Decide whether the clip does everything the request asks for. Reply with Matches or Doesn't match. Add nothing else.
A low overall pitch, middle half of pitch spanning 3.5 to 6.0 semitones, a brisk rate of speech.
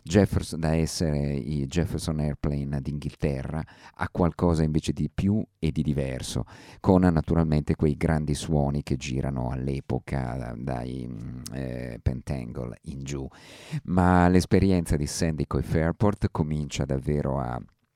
Doesn't match